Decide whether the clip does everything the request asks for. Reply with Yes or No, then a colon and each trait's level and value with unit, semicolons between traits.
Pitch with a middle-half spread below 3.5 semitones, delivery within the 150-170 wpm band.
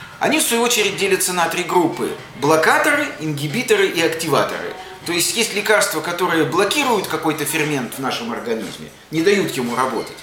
No: wide, 5.4 semitones; fast, 160 wpm